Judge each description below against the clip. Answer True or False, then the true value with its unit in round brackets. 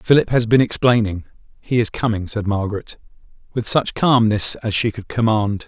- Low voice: True (110 Hz)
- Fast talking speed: False (160 wpm)